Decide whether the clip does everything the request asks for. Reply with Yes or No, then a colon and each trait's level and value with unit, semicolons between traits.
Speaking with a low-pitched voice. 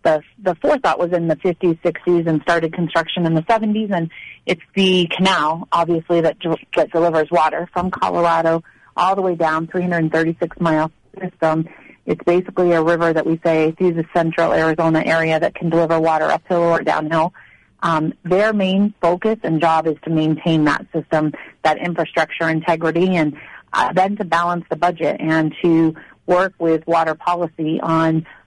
No: medium, 165 Hz